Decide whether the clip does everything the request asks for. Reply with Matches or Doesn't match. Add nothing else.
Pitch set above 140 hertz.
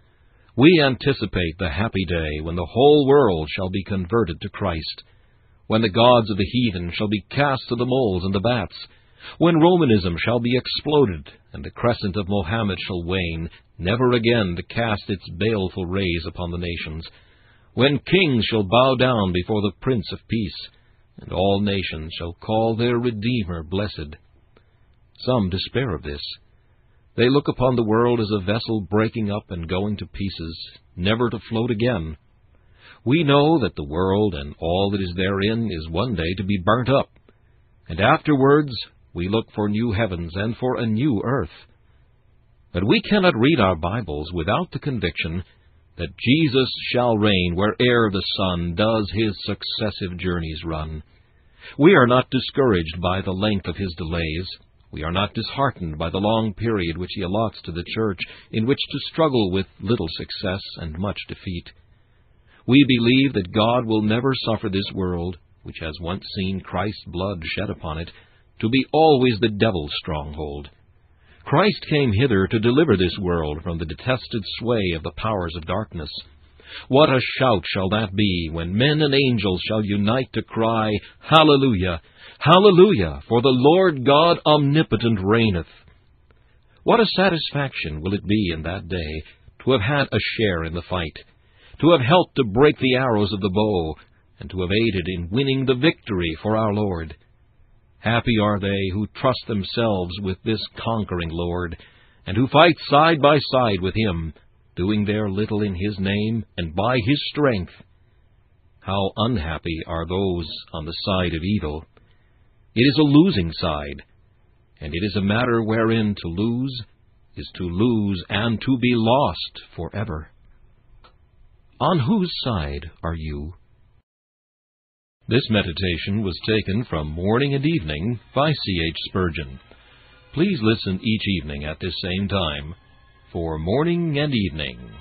Doesn't match